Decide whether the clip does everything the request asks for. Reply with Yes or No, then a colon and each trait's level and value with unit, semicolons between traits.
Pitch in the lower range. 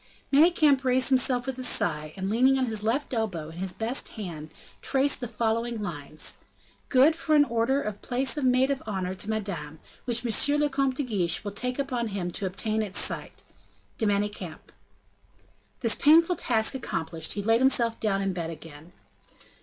No: high, 225 Hz